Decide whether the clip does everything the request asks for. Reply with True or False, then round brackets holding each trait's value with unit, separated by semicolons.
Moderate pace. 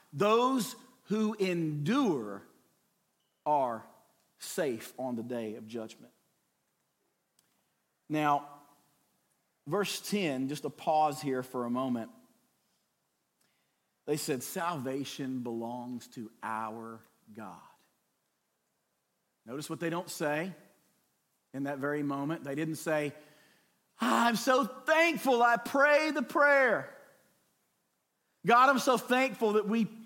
False (105 wpm)